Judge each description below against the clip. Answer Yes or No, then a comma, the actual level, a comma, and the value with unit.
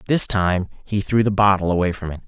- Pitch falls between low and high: No, very low, 95 Hz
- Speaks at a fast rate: Yes, fast, 240 wpm